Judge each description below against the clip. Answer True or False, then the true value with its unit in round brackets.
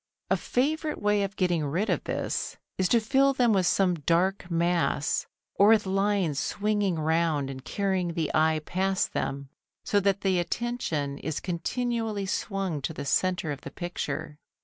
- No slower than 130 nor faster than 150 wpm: False (165 wpm)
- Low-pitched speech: False (185 Hz)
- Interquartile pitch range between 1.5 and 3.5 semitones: False (4.3 semitones)